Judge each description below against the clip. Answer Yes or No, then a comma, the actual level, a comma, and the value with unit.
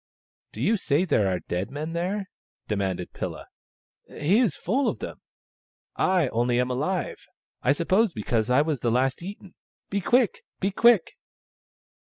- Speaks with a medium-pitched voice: Yes, medium, 155 Hz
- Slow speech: No, average, 170 wpm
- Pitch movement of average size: No, wide, 7.9 semitones